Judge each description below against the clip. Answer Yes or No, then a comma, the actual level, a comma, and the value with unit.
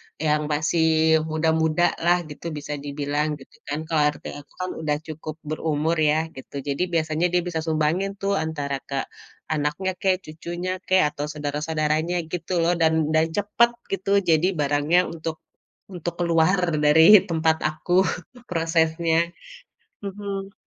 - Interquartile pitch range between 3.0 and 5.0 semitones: No, narrow, 2.6 semitones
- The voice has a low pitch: No, medium, 160 Hz